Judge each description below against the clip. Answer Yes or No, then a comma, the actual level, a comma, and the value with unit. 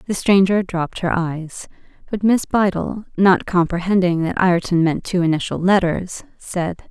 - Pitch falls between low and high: Yes, medium, 180 Hz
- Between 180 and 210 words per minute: No, average, 150 wpm